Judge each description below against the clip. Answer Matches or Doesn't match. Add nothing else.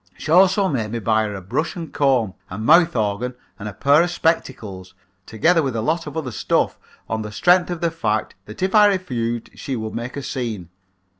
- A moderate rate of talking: Doesn't match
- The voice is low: Matches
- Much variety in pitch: Matches